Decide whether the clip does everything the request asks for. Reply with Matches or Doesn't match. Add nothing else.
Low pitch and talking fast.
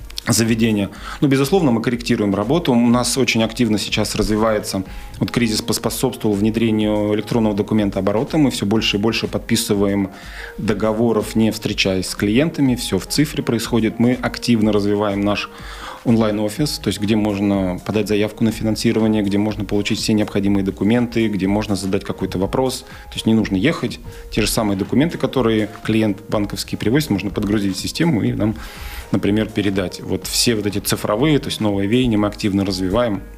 Matches